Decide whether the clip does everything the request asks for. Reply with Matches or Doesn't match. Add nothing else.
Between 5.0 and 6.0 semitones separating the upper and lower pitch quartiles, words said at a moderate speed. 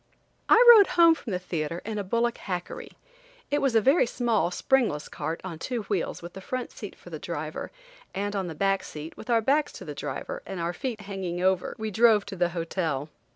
Doesn't match